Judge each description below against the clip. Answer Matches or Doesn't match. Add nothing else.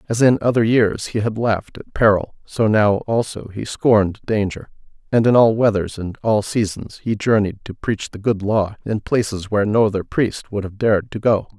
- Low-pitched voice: Matches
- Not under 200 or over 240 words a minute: Matches